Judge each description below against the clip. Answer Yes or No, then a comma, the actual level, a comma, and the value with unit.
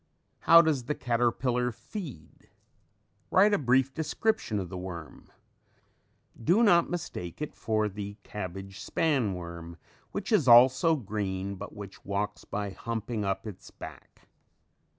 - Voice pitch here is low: Yes, low, 110 Hz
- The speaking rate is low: Yes, slow, 130 wpm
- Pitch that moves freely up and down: Yes, wide, 7.2 semitones